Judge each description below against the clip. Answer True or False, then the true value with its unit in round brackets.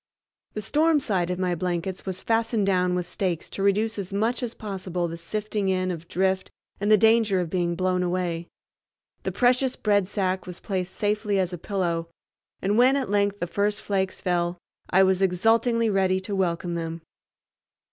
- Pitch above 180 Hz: True (190 Hz)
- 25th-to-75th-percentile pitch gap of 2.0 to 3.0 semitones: True (2.7 semitones)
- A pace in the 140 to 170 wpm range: False (180 wpm)